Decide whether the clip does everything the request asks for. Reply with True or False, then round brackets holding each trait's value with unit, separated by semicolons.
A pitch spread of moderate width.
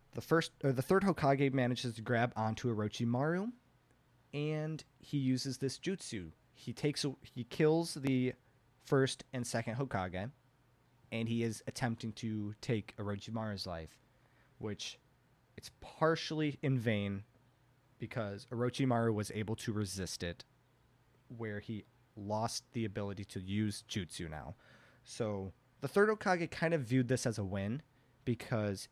True (3.6 semitones)